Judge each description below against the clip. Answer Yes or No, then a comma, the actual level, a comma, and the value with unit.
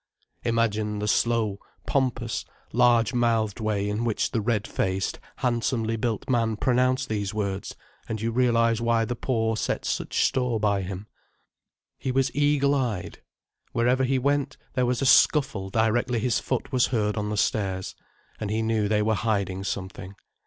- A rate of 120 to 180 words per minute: Yes, average, 160 wpm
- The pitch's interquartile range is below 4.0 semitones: Yes, average, 2.8 semitones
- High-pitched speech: No, low, 115 Hz